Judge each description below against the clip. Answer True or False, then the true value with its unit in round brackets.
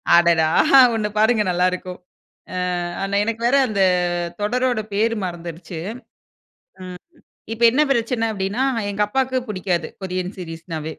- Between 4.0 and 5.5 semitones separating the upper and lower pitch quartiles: True (4.4 semitones)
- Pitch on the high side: True (200 Hz)